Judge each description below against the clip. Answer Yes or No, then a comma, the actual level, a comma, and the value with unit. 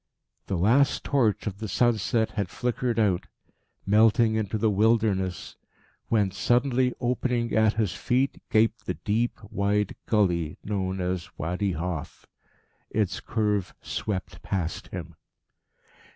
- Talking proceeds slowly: Yes, slow, 125 wpm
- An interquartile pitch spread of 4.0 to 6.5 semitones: No, average, 3.5 semitones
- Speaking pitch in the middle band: No, low, 105 Hz